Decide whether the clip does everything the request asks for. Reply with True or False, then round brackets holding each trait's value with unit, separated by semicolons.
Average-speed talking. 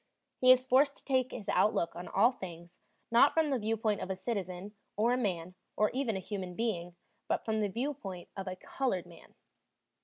True (195 wpm)